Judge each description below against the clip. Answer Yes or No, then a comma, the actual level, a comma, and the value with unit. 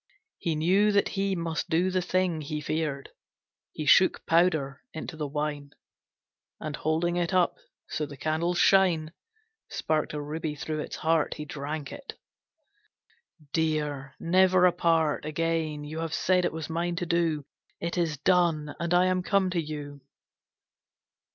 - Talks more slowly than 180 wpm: Yes, average, 150 wpm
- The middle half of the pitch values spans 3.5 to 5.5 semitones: No, average, 2.7 semitones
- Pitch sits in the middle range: Yes, medium, 160 Hz